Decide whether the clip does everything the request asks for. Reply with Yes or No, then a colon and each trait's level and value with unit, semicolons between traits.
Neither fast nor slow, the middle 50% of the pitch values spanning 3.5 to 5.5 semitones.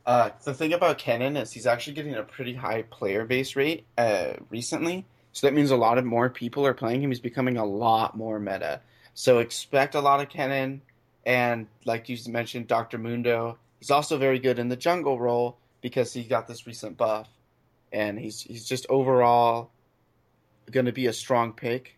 No: average, 195 wpm; narrow, 2.4 semitones